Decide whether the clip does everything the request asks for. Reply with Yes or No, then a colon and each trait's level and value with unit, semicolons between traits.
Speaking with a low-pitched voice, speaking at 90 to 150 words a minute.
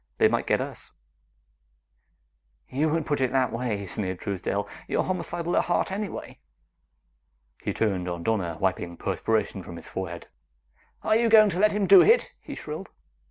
No: low, 125 Hz; average, 160 wpm